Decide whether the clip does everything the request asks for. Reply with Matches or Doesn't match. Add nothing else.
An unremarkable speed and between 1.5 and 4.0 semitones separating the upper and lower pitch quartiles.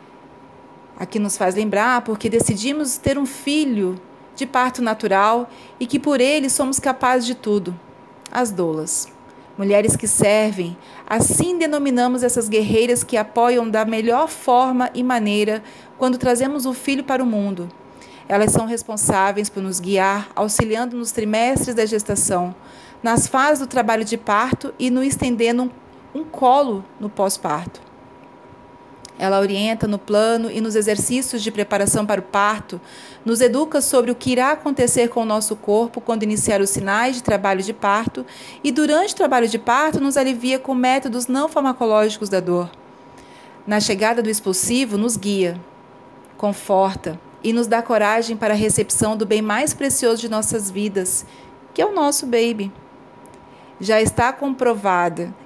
Matches